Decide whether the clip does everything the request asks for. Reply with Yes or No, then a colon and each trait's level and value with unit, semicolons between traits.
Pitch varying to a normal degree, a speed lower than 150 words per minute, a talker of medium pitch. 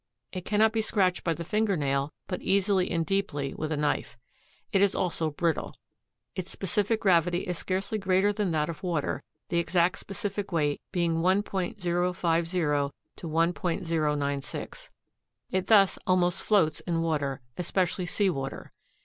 Yes: average, 3.2 semitones; average, 140 wpm; medium, 175 Hz